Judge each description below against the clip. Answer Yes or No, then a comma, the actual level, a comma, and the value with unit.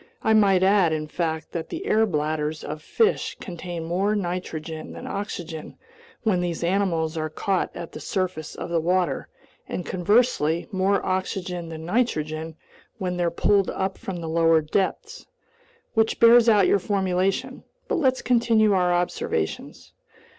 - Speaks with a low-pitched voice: No, medium, 180 Hz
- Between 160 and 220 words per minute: No, average, 150 wpm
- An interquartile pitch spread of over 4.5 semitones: No, average, 3.8 semitones